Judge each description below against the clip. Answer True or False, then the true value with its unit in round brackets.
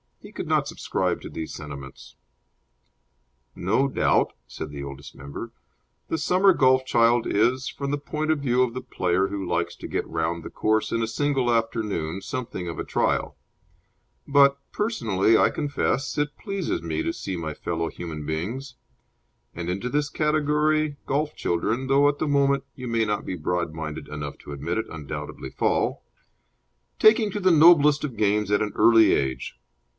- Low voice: True (115 Hz)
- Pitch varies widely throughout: True (8.9 semitones)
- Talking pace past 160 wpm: True (170 wpm)